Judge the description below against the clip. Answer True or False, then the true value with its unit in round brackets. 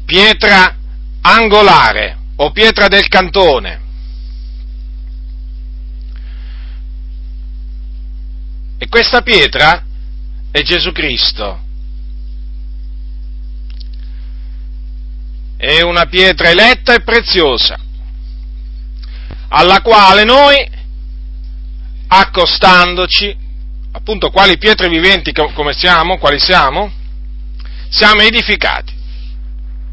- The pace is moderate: False (65 wpm)